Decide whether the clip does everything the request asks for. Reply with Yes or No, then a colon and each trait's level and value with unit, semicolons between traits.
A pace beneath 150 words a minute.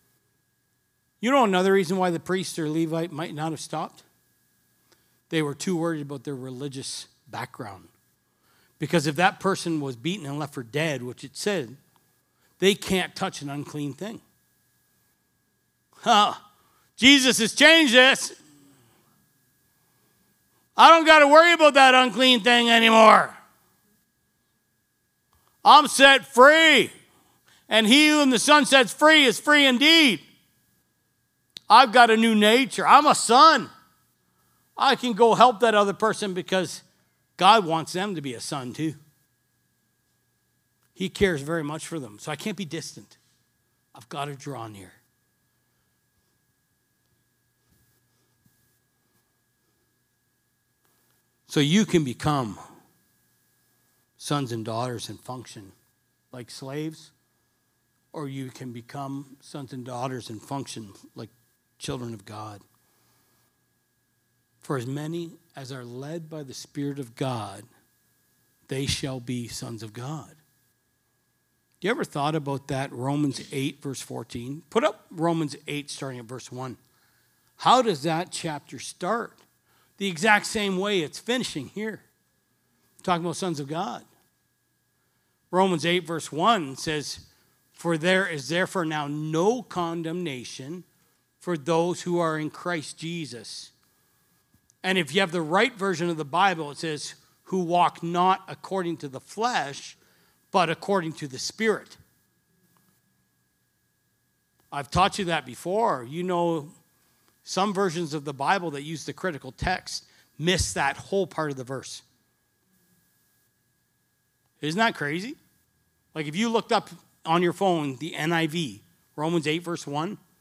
Yes: slow, 135 wpm